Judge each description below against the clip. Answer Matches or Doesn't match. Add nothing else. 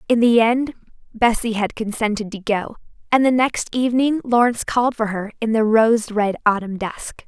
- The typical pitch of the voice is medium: Doesn't match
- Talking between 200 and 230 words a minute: Doesn't match